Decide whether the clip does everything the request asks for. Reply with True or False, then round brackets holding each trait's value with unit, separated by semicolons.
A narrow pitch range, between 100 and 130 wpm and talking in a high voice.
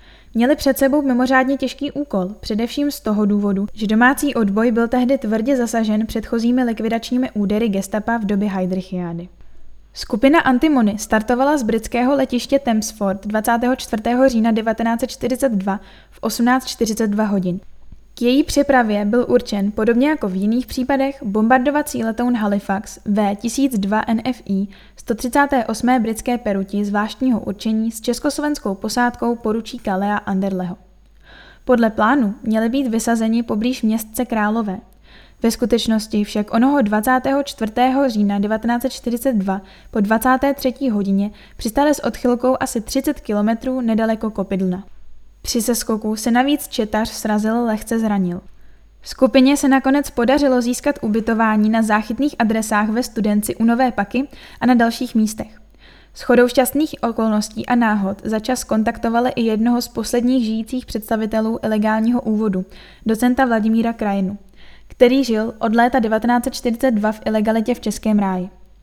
False (3.0 semitones; 125 wpm; 230 Hz)